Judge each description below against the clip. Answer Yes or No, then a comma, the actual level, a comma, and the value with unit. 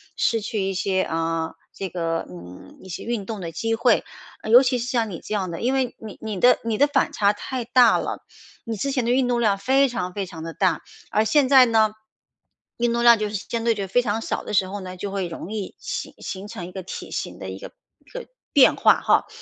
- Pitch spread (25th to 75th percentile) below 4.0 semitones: No, average, 4.3 semitones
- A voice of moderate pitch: No, high, 215 Hz